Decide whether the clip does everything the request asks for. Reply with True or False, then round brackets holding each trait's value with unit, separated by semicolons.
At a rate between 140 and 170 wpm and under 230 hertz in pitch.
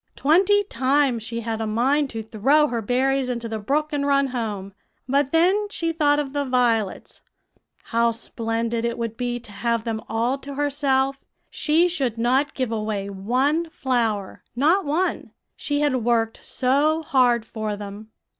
False (165 wpm; 250 Hz)